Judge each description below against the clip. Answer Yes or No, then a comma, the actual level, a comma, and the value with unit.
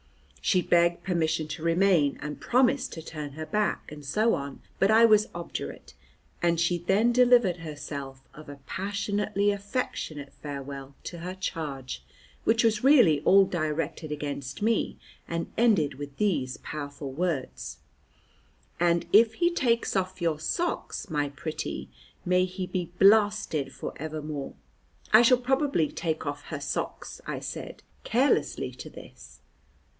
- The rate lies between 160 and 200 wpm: No, average, 140 wpm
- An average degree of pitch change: No, wide, 5.8 semitones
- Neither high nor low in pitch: Yes, medium, 170 Hz